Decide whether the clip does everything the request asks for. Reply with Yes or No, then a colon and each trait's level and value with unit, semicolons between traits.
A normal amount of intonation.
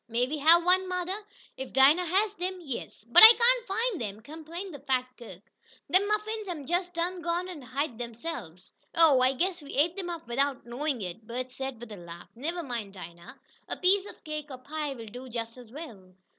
No: wide, 6.9 semitones